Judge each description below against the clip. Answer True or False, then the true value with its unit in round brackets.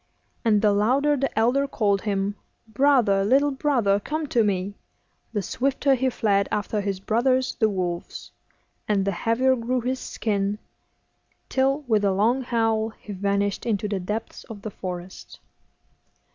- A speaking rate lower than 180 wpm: True (150 wpm)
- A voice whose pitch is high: True (220 Hz)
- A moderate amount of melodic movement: True (4.3 semitones)